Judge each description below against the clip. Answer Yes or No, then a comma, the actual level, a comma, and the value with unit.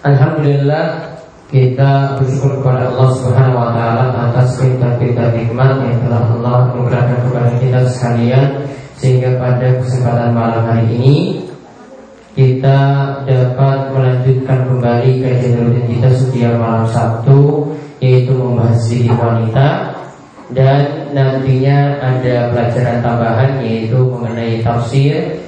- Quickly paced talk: No, average, 110 wpm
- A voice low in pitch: Yes, low, 125 Hz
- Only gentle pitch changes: Yes, narrow, 2.3 semitones